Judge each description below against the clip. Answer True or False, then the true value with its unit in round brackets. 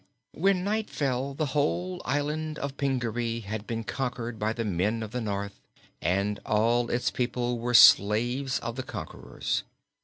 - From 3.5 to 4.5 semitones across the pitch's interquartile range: True (4.1 semitones)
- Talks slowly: False (165 wpm)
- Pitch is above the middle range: False (120 Hz)